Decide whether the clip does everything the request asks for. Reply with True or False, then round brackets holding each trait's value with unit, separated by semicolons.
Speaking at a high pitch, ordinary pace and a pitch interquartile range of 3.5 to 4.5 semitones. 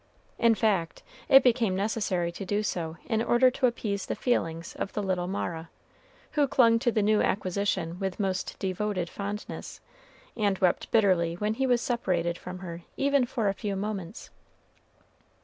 True (200 Hz; 165 wpm; 3.9 semitones)